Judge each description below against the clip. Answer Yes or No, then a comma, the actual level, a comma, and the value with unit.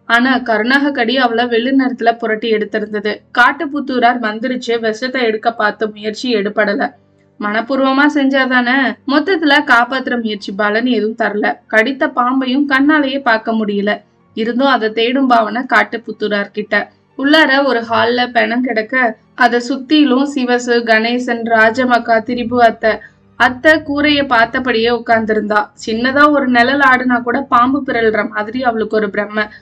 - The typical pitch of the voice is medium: No, high, 240 Hz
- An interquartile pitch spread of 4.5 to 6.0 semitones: No, average, 3.0 semitones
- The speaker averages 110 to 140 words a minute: Yes, average, 115 wpm